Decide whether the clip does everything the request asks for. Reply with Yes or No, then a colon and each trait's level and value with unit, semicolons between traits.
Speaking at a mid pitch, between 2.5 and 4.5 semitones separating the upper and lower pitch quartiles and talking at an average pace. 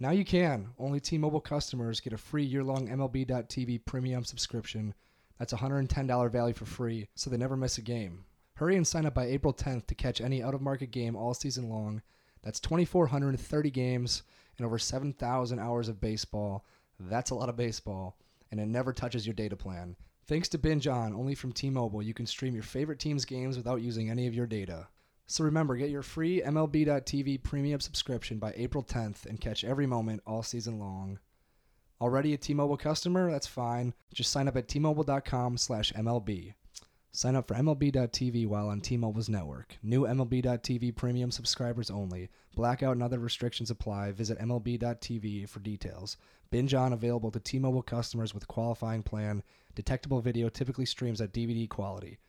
No: low, 120 Hz; average, 3.4 semitones; average, 180 wpm